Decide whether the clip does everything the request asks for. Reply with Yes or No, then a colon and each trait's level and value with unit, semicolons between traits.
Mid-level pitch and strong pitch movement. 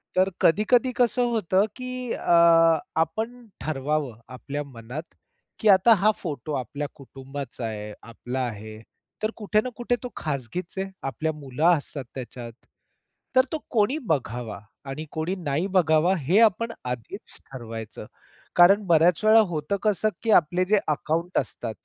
Yes: medium, 160 Hz; wide, 7.5 semitones